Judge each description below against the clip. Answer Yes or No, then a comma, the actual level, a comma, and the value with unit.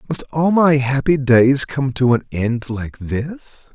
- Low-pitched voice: Yes, low, 130 Hz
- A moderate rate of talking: Yes, average, 175 wpm